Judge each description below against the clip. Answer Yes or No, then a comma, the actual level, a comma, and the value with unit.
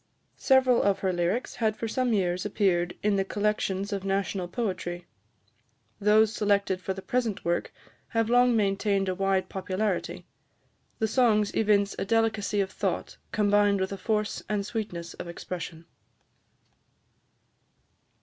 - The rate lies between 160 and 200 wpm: No, average, 140 wpm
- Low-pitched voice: No, high, 200 Hz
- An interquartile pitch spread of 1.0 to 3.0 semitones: Yes, narrow, 2.4 semitones